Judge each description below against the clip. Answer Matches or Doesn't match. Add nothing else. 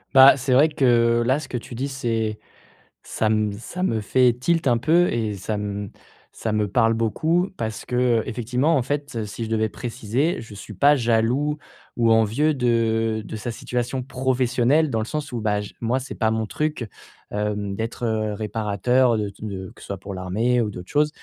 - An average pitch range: Matches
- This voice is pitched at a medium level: Doesn't match